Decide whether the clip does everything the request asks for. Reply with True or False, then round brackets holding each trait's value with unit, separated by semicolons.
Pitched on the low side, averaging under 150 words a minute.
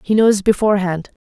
False (200 Hz; 140 wpm)